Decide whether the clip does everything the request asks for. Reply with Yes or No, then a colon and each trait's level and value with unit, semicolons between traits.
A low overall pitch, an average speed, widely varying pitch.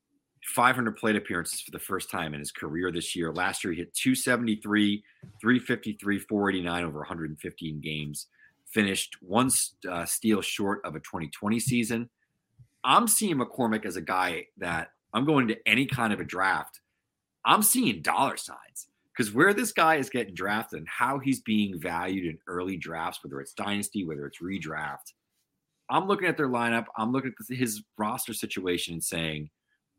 Yes: low, 105 Hz; average, 170 wpm; wide, 6.1 semitones